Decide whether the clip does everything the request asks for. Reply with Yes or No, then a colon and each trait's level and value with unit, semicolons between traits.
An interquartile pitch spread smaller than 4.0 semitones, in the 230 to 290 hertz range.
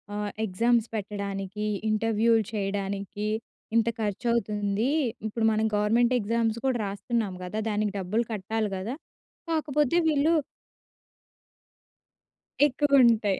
No: narrow, 2.6 semitones; high, 215 Hz